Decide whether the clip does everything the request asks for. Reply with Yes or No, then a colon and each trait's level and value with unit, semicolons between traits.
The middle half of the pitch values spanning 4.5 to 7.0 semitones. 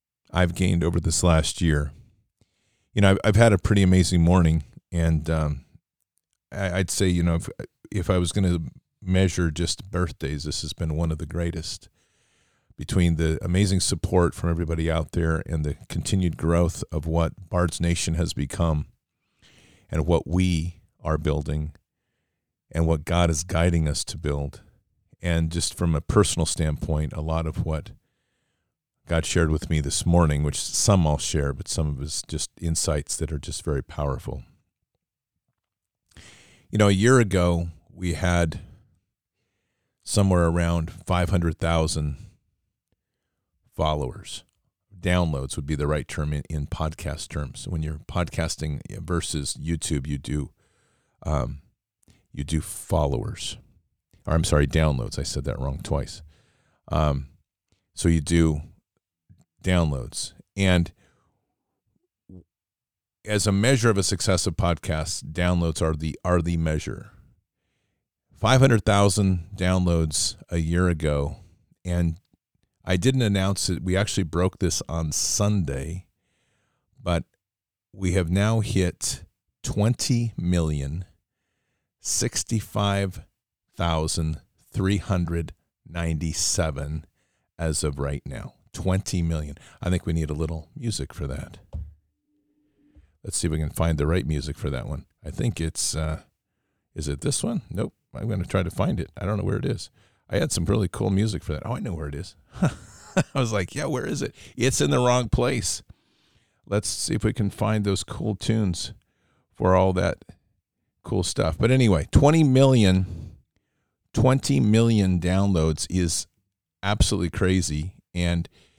No: average, 3.8 semitones